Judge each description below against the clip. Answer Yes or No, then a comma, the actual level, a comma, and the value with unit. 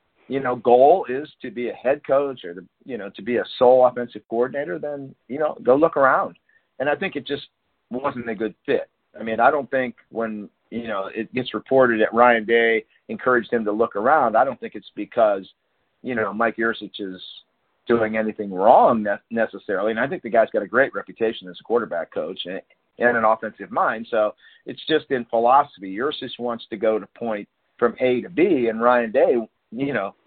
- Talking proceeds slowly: No, fast, 205 wpm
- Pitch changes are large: No, average, 2.7 semitones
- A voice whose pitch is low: Yes, low, 115 Hz